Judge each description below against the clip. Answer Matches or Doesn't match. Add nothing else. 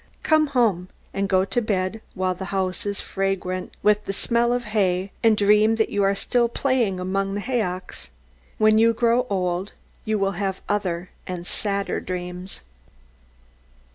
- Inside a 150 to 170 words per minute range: Matches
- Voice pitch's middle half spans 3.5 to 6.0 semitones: Doesn't match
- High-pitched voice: Matches